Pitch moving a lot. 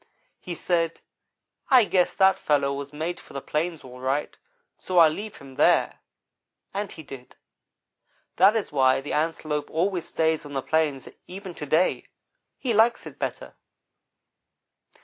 No: average, 4.5 semitones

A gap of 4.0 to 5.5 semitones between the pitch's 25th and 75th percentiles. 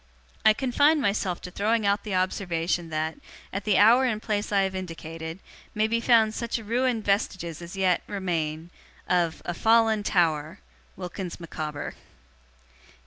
Yes: average, 4.3 semitones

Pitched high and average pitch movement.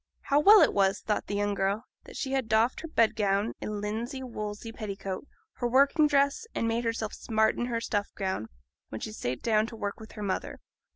Yes: high, 220 Hz; average, 3.0 semitones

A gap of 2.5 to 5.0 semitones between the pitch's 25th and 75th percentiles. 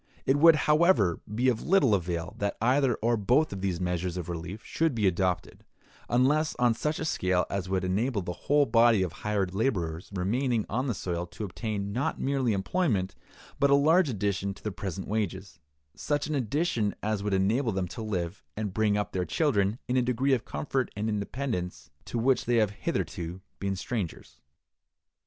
No: wide, 5.5 semitones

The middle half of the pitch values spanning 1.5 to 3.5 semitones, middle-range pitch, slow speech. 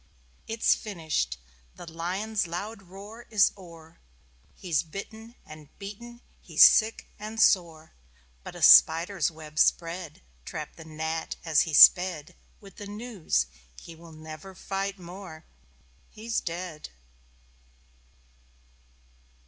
No: average, 4.2 semitones; medium, 175 Hz; slow, 110 wpm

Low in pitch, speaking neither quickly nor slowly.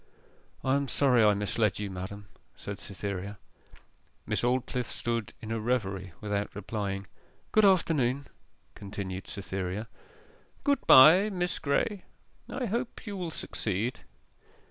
No: low, 115 Hz; slow, 120 wpm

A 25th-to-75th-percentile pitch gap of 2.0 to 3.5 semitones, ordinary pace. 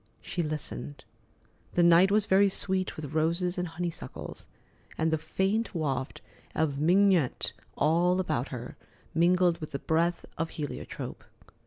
No: average, 2.8 semitones; slow, 130 wpm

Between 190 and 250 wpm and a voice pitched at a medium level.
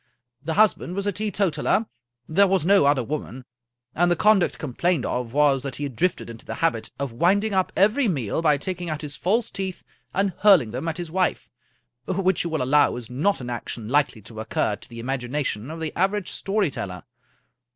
Yes: average, 200 wpm; medium, 160 Hz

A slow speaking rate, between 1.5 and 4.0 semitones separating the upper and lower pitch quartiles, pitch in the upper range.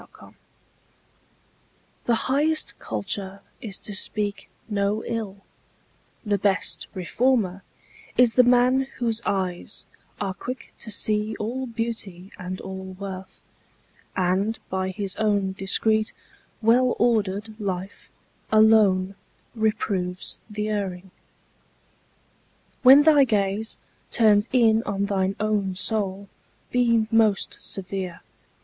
Yes: slow, 105 wpm; average, 3.0 semitones; high, 210 Hz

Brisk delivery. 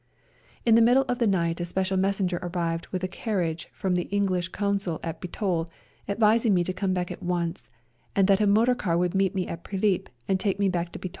Yes: fast, 225 wpm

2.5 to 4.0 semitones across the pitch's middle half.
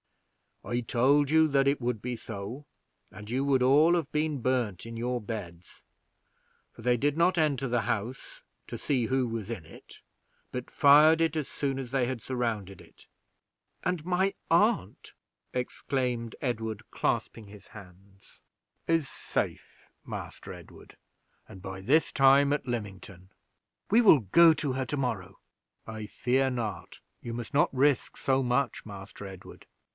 No: average, 4.5 semitones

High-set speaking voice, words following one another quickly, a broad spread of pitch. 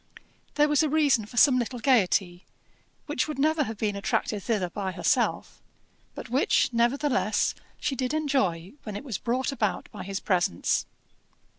No: high, 240 Hz; average, 160 wpm; wide, 5.7 semitones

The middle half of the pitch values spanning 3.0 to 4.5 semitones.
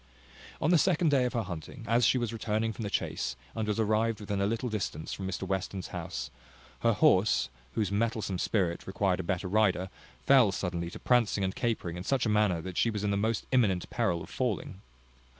Yes: average, 3.5 semitones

